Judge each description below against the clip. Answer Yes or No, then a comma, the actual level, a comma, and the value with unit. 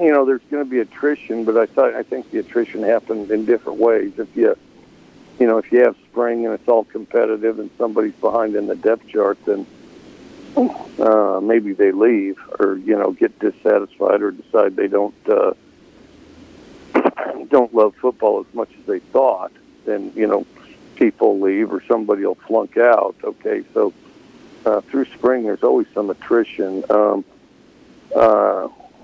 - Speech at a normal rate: Yes, average, 165 wpm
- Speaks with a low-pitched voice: Yes, low, 125 Hz